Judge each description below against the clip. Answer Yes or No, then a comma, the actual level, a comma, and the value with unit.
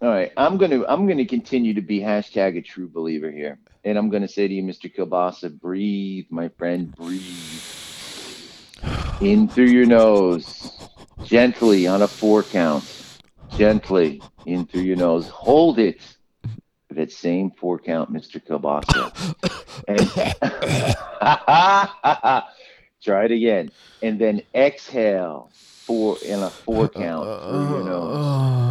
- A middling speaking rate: No, slow, 130 wpm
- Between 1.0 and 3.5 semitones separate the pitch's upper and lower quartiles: No, average, 4.7 semitones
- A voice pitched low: Yes, low, 100 Hz